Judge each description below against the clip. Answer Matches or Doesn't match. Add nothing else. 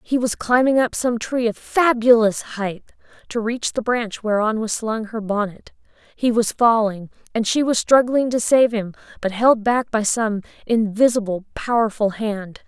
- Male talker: Doesn't match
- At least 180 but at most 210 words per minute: Doesn't match